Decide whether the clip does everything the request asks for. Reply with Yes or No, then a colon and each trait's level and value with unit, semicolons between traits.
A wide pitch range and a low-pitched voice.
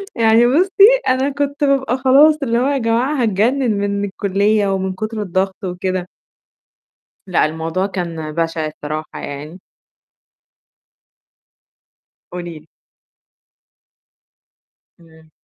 No: wide, 7.0 semitones; high, 200 Hz